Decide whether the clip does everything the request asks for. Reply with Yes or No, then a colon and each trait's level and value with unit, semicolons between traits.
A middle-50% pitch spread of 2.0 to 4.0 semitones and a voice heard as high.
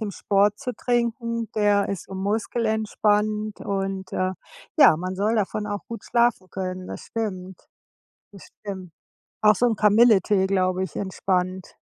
Yes: narrow, 2.6 semitones; high, 205 Hz